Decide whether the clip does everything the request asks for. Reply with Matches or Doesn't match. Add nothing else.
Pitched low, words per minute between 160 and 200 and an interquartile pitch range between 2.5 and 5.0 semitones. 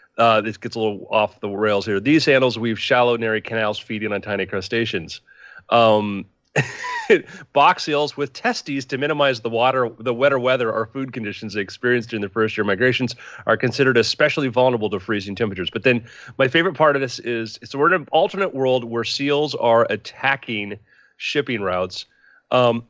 Matches